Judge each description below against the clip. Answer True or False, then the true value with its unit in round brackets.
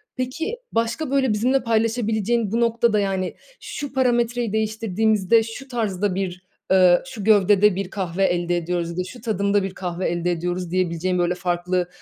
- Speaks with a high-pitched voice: True (200 Hz)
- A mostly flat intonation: False (4.1 semitones)